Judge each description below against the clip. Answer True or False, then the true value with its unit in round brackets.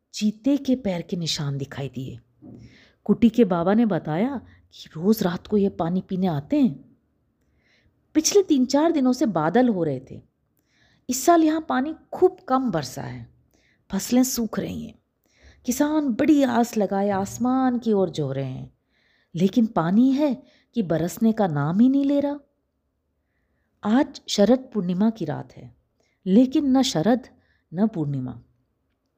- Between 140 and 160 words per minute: True (150 wpm)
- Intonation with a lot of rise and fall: True (8.8 semitones)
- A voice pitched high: True (205 Hz)